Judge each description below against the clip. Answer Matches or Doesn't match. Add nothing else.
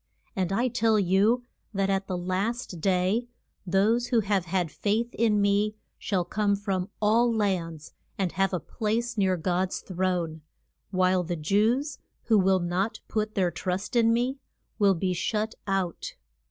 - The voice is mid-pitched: Doesn't match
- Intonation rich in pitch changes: Doesn't match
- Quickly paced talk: Doesn't match